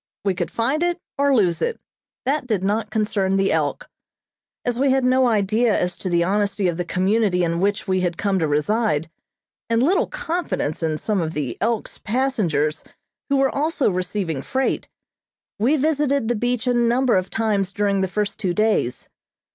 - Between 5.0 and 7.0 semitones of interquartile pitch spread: Yes, wide, 5.5 semitones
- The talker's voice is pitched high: Yes, high, 210 Hz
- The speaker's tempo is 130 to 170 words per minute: No, average, 180 wpm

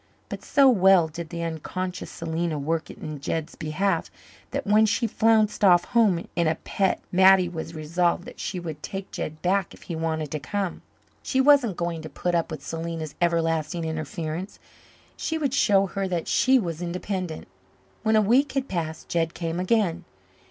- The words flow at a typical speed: Yes, average, 175 wpm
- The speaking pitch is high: No, medium, 175 Hz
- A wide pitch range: No, average, 3.5 semitones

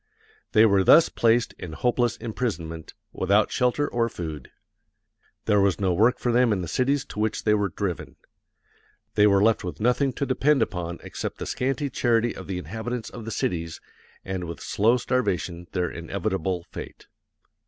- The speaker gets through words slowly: No, average, 170 wpm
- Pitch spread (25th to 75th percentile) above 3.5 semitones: Yes, average, 5.1 semitones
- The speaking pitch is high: No, low, 105 Hz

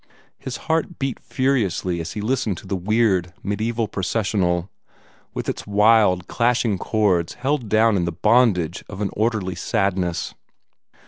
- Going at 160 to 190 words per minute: No, average, 140 wpm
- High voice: No, low, 105 Hz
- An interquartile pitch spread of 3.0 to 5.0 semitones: Yes, average, 4.2 semitones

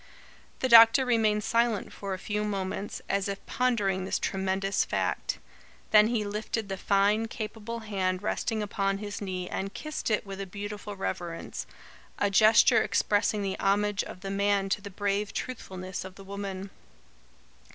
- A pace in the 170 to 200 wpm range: No, average, 160 wpm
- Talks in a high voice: Yes, high, 200 Hz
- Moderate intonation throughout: No, narrow, 1.6 semitones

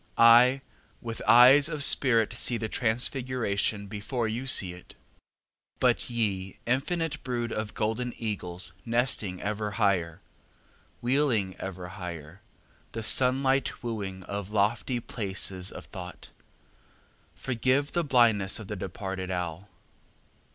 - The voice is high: No, low, 110 Hz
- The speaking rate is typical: No, slow, 120 wpm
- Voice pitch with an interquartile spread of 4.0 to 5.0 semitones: Yes, average, 4.4 semitones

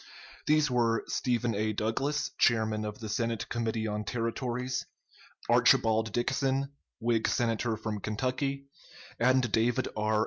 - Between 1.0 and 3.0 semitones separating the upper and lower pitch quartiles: Yes, average, 2.7 semitones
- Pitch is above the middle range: No, low, 115 Hz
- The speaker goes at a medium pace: No, slow, 125 wpm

